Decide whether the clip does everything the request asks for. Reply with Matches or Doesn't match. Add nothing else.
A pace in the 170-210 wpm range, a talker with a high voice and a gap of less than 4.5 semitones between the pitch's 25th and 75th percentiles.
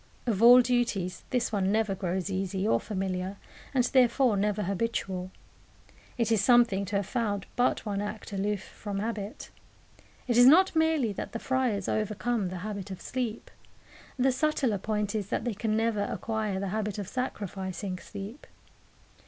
Doesn't match